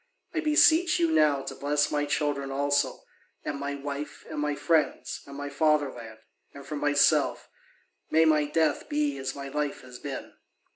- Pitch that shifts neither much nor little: No, narrow, 1.4 semitones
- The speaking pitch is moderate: Yes, medium, 145 Hz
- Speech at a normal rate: Yes, average, 165 wpm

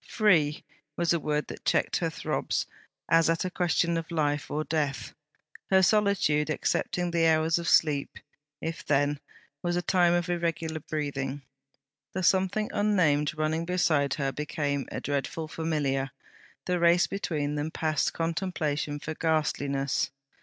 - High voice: No, medium, 160 Hz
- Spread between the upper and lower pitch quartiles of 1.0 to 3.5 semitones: Yes, average, 2.8 semitones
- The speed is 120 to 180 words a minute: Yes, average, 145 wpm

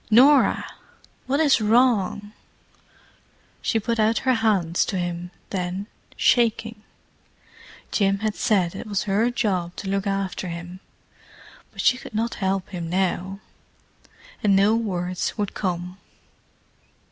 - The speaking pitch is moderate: No, high, 200 Hz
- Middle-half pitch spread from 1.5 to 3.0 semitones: No, average, 3.4 semitones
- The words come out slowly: Yes, slow, 125 wpm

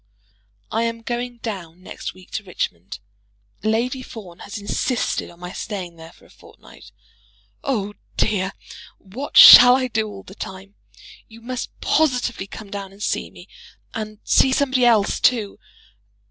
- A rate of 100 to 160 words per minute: Yes, average, 150 wpm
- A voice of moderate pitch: No, high, 215 Hz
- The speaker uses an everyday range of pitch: Yes, average, 4.1 semitones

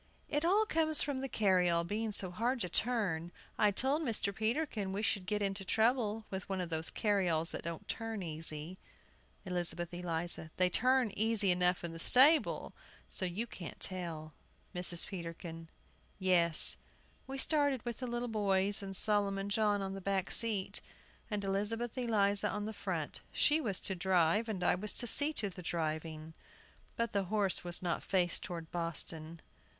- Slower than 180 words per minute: Yes, average, 170 wpm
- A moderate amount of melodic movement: Yes, average, 4.3 semitones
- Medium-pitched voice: No, high, 195 Hz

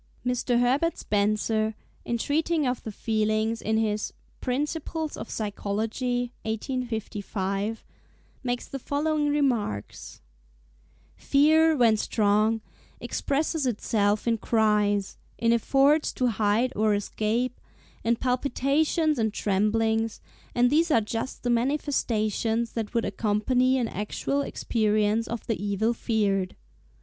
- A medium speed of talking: No, slow, 110 wpm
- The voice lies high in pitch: Yes, high, 225 Hz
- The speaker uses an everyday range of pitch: Yes, average, 3.4 semitones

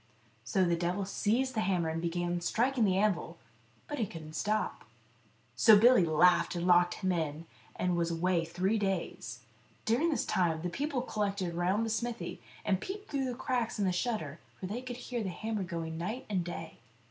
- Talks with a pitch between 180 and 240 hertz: Yes, high, 190 Hz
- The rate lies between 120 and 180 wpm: No, average, 190 wpm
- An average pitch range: Yes, average, 4.7 semitones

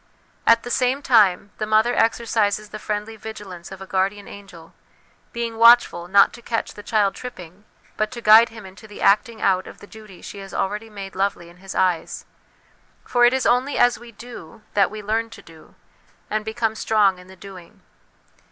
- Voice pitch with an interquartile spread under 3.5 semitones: Yes, average, 2.9 semitones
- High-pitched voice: Yes, high, 210 Hz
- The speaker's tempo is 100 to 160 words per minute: No, average, 190 wpm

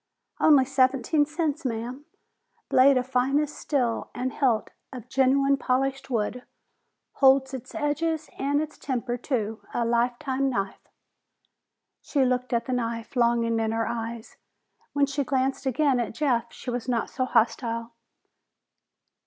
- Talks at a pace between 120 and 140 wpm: Yes, slow, 135 wpm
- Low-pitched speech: No, very high, 255 Hz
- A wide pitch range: No, average, 2.7 semitones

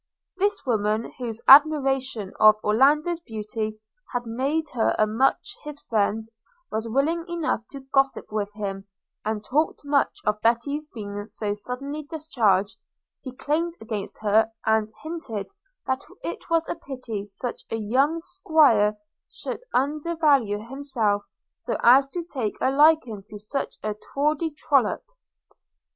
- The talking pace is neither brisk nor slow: No, slow, 130 wpm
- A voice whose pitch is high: Yes, very high, 250 Hz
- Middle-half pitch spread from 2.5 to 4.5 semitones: No, wide, 5.6 semitones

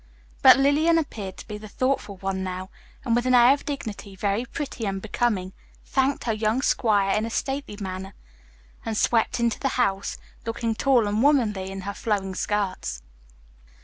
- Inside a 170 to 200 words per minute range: Yes, average, 175 wpm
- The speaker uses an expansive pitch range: No, average, 4.4 semitones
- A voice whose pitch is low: No, high, 215 Hz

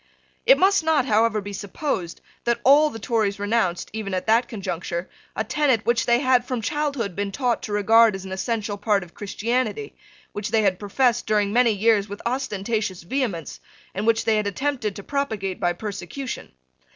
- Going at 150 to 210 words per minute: Yes, average, 180 wpm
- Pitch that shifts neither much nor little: Yes, average, 3.7 semitones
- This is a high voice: Yes, high, 220 Hz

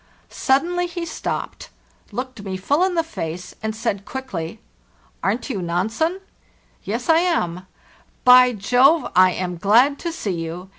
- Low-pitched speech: No, high, 230 Hz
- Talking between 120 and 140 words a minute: No, average, 155 wpm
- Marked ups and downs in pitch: Yes, wide, 9.0 semitones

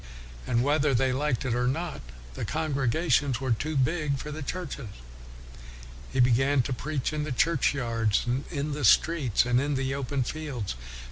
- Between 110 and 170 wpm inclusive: Yes, average, 165 wpm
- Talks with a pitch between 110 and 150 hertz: Yes, low, 135 Hz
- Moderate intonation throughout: Yes, average, 3.3 semitones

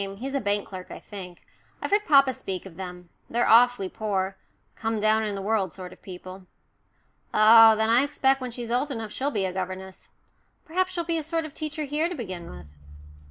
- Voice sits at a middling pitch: No, high, 220 Hz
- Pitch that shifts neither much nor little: No, wide, 6.4 semitones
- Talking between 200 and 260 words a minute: Yes, fast, 205 wpm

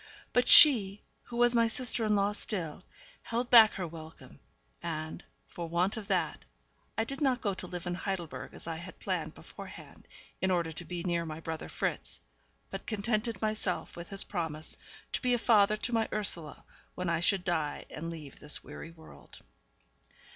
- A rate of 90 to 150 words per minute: No, average, 180 wpm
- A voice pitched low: No, medium, 185 Hz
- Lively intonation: No, average, 4.9 semitones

